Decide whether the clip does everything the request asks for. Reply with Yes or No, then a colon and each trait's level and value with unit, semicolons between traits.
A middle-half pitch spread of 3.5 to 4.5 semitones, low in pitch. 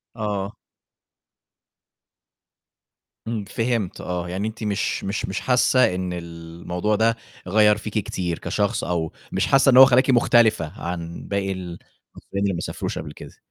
Yes: average, 4.1 semitones; low, 100 Hz